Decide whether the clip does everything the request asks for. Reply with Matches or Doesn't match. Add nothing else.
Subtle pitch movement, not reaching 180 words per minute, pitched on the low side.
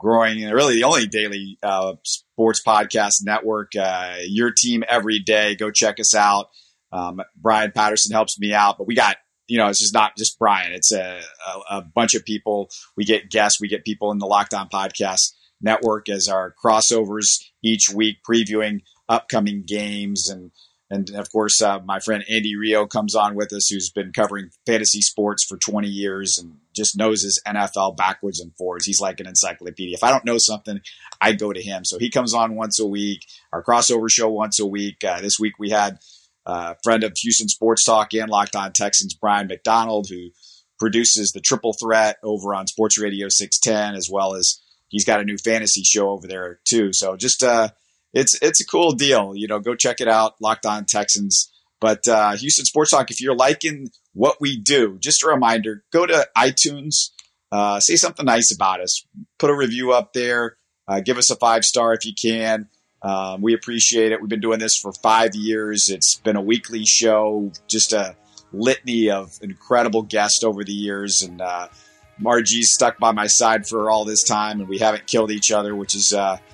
Doesn't match